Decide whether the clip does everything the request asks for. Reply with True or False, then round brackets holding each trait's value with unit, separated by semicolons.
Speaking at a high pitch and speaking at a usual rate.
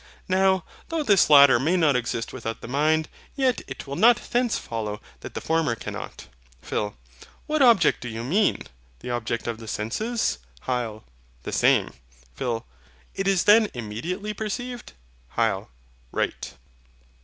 False (155 Hz; 145 wpm)